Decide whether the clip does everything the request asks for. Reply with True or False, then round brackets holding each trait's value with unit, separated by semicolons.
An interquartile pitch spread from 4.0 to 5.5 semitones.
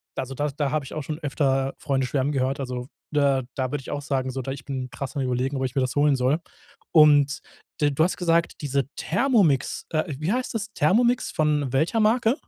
False (2.7 semitones)